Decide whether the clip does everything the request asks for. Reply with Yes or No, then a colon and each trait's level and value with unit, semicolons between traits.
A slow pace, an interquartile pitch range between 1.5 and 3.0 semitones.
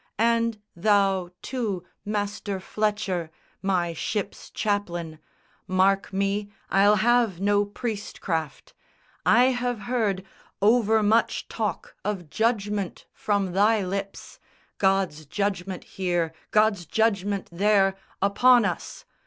Yes: slow, 105 wpm; narrow, 2.4 semitones